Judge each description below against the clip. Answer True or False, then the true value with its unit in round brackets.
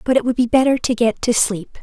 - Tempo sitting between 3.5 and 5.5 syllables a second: False (5.9 syllables/s)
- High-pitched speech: True (240 Hz)